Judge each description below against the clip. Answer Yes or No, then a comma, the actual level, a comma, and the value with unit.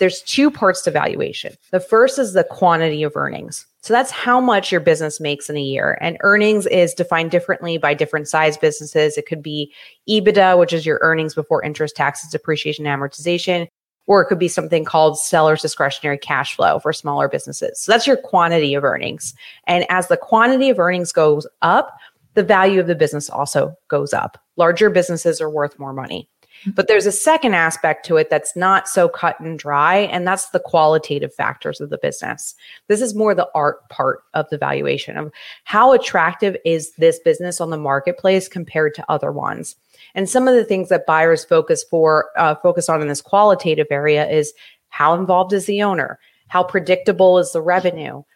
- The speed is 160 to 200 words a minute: Yes, average, 195 wpm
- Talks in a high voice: No, medium, 175 Hz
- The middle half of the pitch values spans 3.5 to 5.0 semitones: Yes, average, 4.0 semitones